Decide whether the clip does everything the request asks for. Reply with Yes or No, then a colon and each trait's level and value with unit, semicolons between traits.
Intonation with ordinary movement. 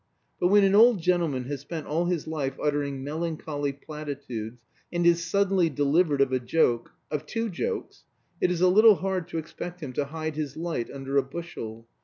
Yes: average, 4.0 semitones